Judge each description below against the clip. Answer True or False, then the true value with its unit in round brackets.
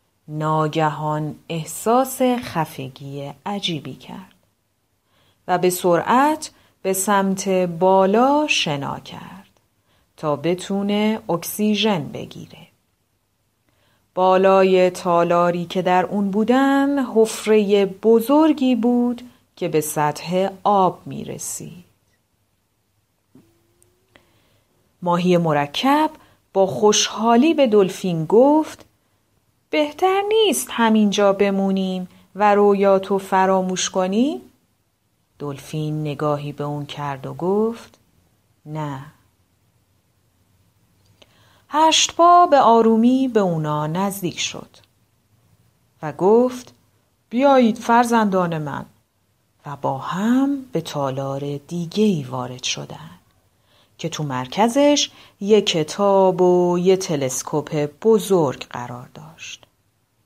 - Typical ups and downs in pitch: False (8.0 semitones)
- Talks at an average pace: False (90 wpm)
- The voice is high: False (180 Hz)